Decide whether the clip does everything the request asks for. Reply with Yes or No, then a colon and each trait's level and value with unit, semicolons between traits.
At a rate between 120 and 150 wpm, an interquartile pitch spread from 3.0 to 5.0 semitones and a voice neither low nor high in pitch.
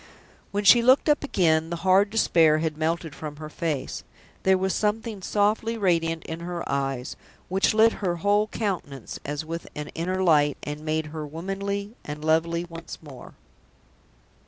No: average, 160 wpm; average, 4.3 semitones; medium, 170 Hz